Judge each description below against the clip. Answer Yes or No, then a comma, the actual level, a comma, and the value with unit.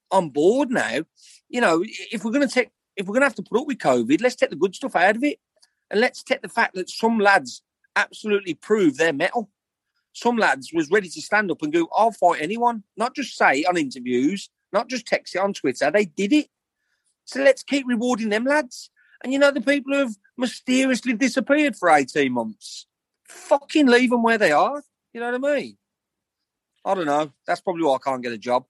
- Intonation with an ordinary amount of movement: No, wide, 5.7 semitones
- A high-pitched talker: Yes, high, 240 Hz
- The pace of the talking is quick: Yes, fast, 225 wpm